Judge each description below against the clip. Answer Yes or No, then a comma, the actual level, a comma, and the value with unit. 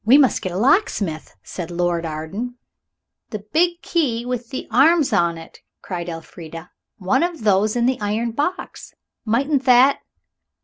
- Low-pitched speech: No, high, 225 Hz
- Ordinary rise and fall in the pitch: No, wide, 7.0 semitones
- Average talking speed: Yes, average, 150 wpm